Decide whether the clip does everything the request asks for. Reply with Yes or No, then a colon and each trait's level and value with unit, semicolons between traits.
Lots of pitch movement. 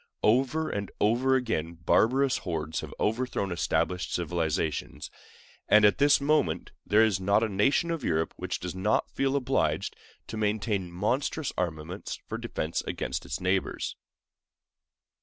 Yes: wide, 6.5 semitones